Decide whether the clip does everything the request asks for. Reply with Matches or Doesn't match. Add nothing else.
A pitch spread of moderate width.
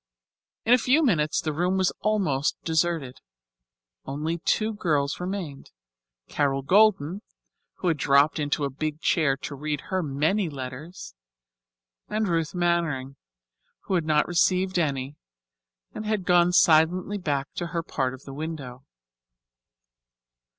Matches